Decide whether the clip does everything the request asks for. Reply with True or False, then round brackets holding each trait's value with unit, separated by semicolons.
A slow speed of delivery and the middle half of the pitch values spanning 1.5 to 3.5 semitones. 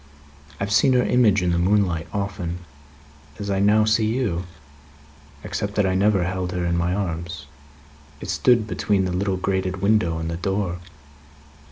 False (170 wpm; 2.9 semitones)